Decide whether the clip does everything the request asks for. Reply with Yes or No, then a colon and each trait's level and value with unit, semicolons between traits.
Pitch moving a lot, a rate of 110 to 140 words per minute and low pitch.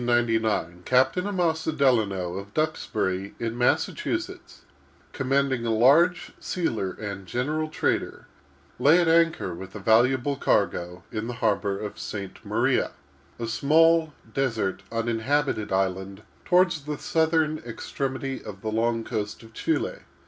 Yes: wide, 6.6 semitones; slow, 135 wpm; low, 120 Hz